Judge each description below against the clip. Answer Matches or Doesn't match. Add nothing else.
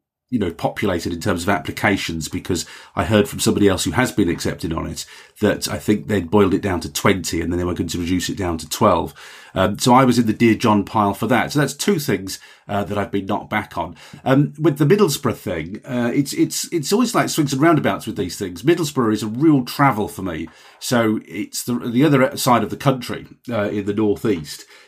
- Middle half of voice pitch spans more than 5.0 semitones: Matches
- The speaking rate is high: Matches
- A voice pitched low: Matches